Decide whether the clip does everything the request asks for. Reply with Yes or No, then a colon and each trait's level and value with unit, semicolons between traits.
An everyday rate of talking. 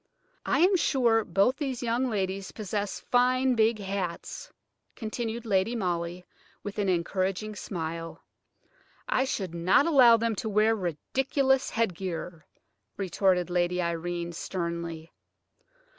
No: slow, 115 wpm